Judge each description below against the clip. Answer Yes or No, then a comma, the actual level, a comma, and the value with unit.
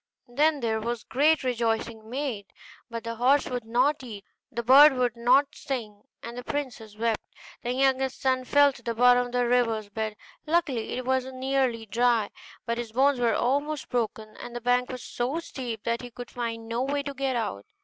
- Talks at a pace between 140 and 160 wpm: No, average, 195 wpm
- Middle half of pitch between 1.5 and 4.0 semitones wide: Yes, narrow, 2.5 semitones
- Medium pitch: No, high, 245 Hz